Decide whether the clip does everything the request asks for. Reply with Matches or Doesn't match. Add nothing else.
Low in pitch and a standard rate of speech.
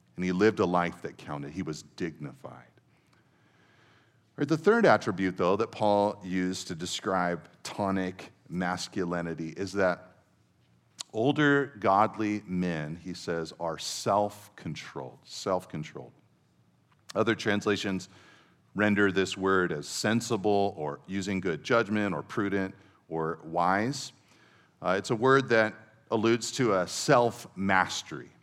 Doesn't match